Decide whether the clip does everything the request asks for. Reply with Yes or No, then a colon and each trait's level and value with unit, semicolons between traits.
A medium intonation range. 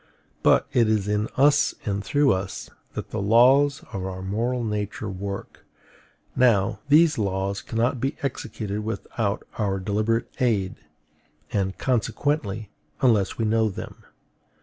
Yes: average, 3.8 semitones